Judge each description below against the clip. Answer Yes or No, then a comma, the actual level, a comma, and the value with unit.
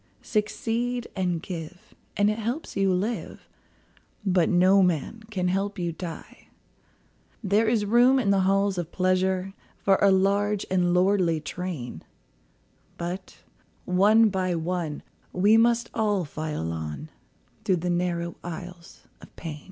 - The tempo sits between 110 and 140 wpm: Yes, slow, 135 wpm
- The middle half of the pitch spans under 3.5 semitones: Yes, average, 2.8 semitones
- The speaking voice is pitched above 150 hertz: Yes, medium, 185 Hz